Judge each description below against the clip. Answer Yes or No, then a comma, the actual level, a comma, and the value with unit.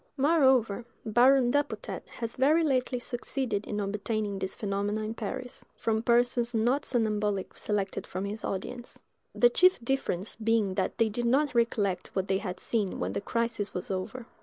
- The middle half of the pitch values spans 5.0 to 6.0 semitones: No, average, 3.6 semitones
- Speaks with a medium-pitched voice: No, high, 225 Hz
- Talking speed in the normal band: Yes, average, 160 wpm